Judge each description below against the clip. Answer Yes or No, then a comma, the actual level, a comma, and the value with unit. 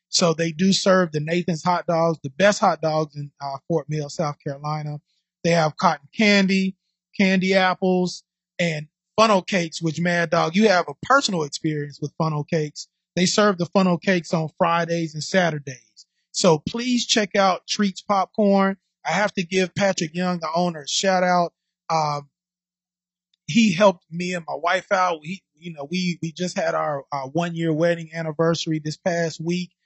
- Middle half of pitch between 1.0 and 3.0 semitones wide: Yes, average, 2.7 semitones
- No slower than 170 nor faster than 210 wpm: Yes, average, 175 wpm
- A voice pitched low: No, medium, 175 Hz